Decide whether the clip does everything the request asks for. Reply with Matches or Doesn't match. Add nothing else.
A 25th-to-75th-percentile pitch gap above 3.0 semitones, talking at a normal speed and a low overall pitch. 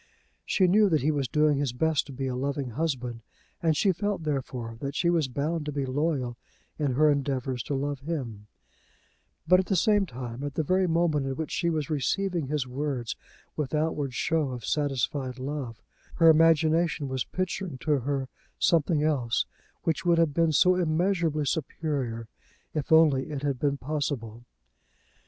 Doesn't match